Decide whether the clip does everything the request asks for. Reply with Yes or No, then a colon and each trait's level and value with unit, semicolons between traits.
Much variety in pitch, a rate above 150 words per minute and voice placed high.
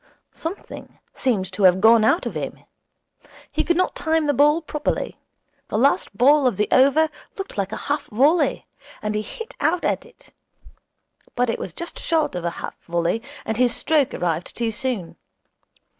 Yes: wide, 7.0 semitones; average, 175 wpm; very high, 255 Hz